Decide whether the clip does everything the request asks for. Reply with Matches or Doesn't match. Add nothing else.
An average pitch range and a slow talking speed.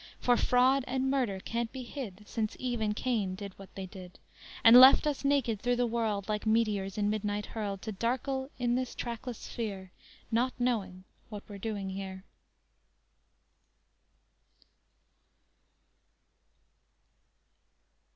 Matches